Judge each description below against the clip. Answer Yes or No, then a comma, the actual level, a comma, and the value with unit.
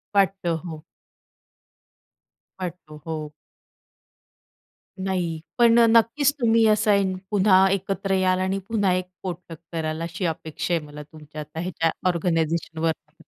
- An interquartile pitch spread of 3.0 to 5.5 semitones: Yes, average, 3.4 semitones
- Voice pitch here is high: No, medium, 180 Hz